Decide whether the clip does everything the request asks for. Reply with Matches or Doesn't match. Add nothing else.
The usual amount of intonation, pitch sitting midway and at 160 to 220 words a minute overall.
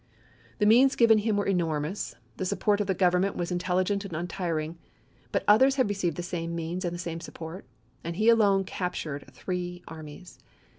Matches